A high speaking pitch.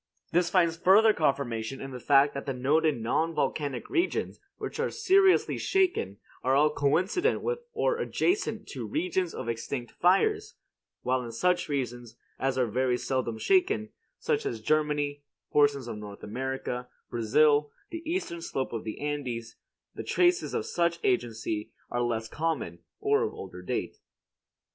No: medium, 145 Hz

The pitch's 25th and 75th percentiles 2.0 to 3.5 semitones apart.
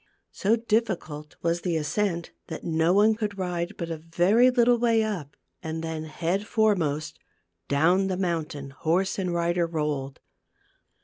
No: average, 4.3 semitones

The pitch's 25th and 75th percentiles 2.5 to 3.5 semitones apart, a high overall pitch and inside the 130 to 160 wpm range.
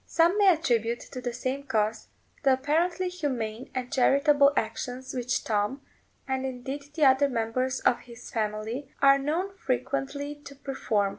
Yes: average, 3.1 semitones; very high, 265 Hz; average, 150 wpm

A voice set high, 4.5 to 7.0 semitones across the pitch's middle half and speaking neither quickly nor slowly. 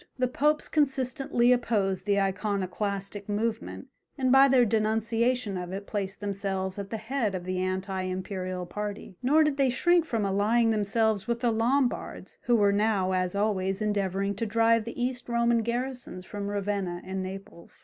No: high, 210 Hz; average, 3.6 semitones; average, 165 wpm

